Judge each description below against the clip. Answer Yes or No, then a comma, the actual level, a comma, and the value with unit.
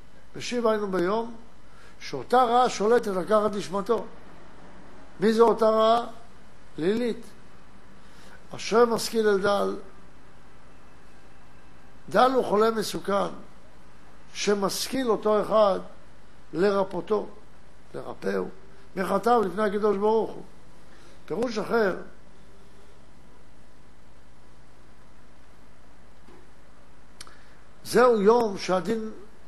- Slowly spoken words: Yes, slow, 70 wpm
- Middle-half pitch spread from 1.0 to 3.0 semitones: No, average, 3.8 semitones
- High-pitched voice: Yes, high, 210 Hz